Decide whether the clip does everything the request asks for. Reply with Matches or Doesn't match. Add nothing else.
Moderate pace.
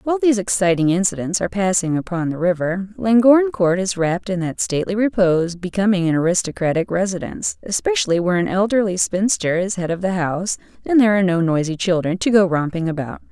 Matches